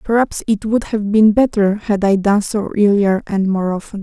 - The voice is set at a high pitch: Yes, high, 205 Hz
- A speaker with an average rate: No, fast, 210 wpm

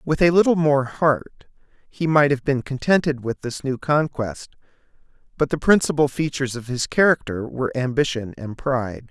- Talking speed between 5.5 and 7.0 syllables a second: No, 5.1 syllables/s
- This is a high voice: No, low, 135 Hz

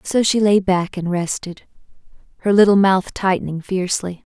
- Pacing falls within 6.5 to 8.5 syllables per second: No, 5.0 syllables/s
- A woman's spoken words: Yes, female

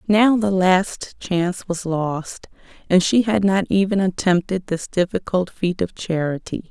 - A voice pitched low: No, medium, 185 Hz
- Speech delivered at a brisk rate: No, average, 150 wpm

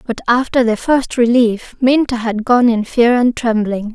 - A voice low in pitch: No, high, 235 Hz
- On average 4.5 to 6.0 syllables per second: No, 4.3 syllables/s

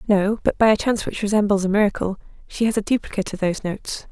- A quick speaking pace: Yes, fast, 235 wpm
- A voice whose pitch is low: No, high, 205 Hz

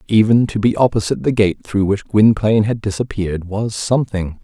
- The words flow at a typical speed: Yes, average, 175 wpm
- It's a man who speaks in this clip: Yes, male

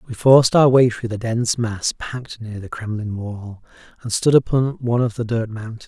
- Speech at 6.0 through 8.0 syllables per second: No, 5.3 syllables/s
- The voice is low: Yes, low, 115 Hz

